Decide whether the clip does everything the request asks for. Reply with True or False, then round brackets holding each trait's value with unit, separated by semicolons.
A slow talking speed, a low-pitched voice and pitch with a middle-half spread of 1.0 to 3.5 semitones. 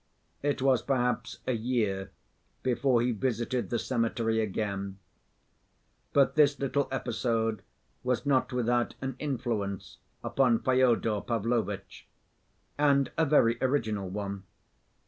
True (105 wpm; 120 Hz; 3.1 semitones)